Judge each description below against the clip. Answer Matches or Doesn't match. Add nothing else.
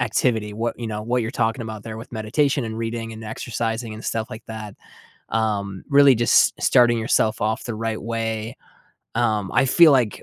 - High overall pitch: Doesn't match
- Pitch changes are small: Matches